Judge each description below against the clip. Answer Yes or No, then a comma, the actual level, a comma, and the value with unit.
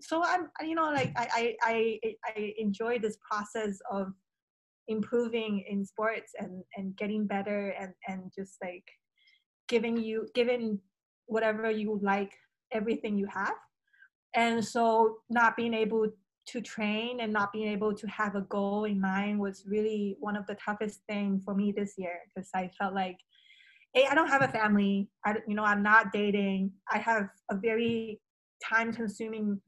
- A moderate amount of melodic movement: No, narrow, 2.3 semitones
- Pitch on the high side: Yes, high, 215 Hz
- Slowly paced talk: No, average, 165 wpm